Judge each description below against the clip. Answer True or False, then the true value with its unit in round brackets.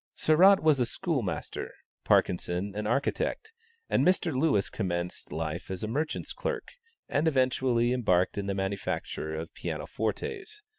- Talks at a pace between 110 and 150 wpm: True (140 wpm)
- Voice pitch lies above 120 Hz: False (115 Hz)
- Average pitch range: False (8.6 semitones)